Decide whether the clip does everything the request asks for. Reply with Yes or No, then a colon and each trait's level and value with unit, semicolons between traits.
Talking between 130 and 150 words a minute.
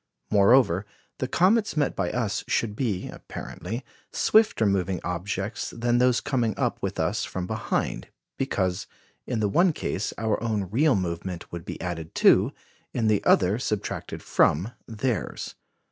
Yes: average, 145 wpm